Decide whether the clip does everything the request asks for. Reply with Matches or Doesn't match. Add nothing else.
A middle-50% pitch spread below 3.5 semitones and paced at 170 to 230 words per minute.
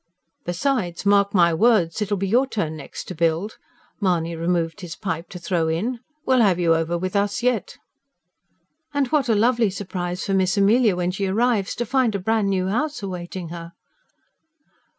Doesn't match